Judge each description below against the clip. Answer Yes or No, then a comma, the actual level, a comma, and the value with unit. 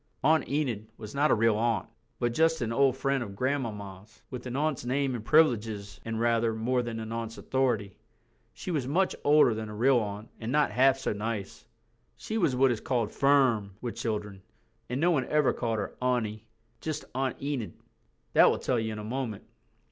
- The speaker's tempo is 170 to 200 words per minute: Yes, average, 195 wpm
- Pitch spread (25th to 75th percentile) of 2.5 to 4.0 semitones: Yes, average, 3.7 semitones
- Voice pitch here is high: No, low, 120 Hz